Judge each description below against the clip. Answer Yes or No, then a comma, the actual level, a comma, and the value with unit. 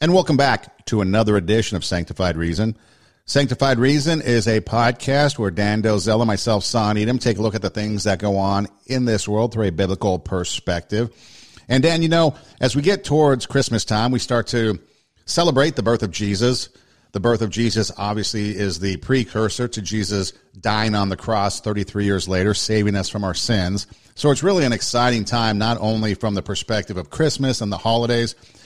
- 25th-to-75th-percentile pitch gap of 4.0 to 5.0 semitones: No, average, 3.4 semitones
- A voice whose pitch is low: Yes, low, 110 Hz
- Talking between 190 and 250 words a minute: Yes, average, 195 wpm